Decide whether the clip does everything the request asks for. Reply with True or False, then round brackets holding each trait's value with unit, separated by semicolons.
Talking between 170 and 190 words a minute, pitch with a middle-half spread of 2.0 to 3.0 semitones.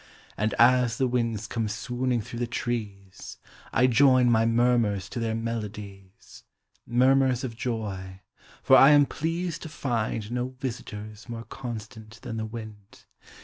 False (150 wpm; 2.7 semitones)